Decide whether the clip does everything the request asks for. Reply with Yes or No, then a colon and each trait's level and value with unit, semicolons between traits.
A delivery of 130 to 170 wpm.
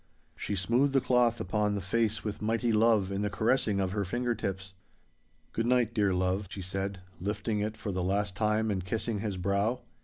No: average, 195 wpm